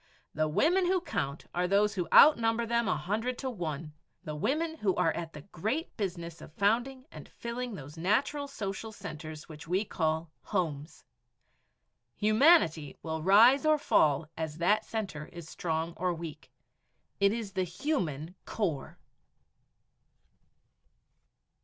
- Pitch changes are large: Yes, wide, 6.6 semitones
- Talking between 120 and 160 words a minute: Yes, average, 140 wpm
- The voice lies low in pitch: No, high, 190 Hz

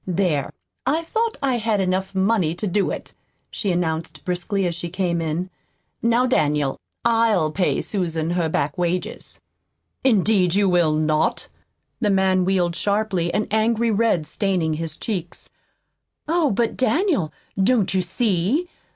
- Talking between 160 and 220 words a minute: No, average, 140 wpm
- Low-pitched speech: No, high, 190 Hz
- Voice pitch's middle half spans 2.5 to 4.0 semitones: No, average, 4.4 semitones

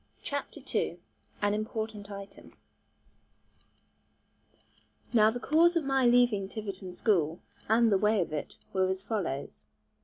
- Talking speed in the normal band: No, slow, 125 wpm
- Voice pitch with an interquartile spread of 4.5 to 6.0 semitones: No, average, 3.7 semitones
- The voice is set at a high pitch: Yes, high, 210 Hz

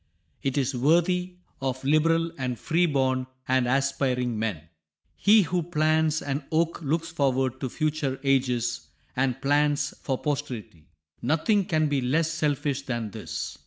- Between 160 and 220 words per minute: No, slow, 135 wpm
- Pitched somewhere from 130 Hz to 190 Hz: Yes, medium, 140 Hz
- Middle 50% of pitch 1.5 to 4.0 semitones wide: Yes, average, 3.6 semitones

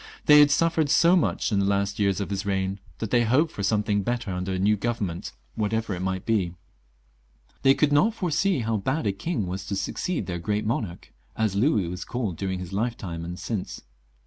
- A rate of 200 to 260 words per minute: Yes, fast, 205 wpm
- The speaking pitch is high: No, low, 105 Hz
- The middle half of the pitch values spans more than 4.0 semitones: Yes, average, 4.7 semitones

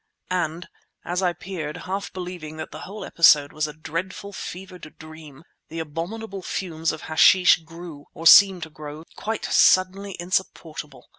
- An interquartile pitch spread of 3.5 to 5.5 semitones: No, average, 3.0 semitones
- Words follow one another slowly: No, average, 150 wpm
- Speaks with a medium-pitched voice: Yes, medium, 170 Hz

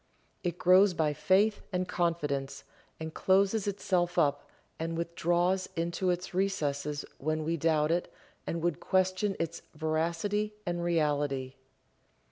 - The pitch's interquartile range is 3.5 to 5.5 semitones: No, average, 3.0 semitones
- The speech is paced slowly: Yes, slow, 125 wpm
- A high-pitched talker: No, medium, 170 Hz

